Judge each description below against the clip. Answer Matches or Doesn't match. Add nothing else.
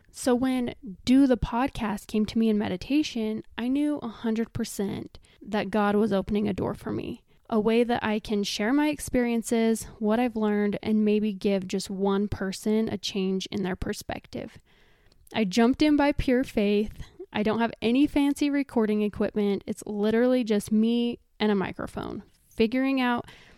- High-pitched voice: Matches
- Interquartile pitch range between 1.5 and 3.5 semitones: Matches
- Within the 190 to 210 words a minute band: Doesn't match